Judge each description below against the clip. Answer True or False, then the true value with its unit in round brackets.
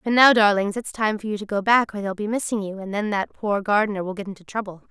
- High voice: True (205 Hz)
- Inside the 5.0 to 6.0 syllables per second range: False (6.3 syllables/s)